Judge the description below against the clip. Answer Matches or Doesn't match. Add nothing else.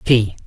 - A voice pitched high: Doesn't match